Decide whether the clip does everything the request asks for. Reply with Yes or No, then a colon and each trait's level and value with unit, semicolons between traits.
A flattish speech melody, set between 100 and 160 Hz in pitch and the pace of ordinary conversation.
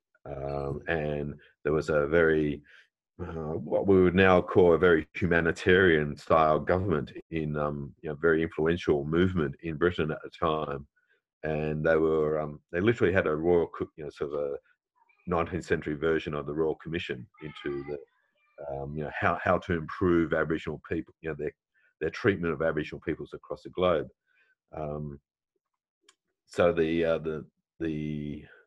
No: narrow, 2.1 semitones; very low, 80 Hz; average, 165 wpm